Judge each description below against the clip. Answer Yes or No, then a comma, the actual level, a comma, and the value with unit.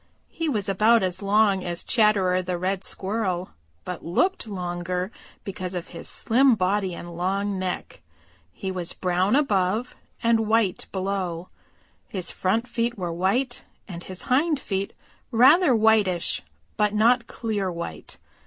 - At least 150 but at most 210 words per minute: No, average, 140 wpm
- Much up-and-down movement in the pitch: No, average, 3.7 semitones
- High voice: Yes, high, 195 Hz